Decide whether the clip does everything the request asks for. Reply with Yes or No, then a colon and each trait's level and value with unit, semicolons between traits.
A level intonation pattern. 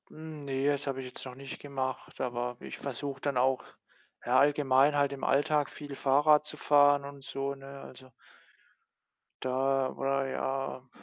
Yes: narrow, 1.3 semitones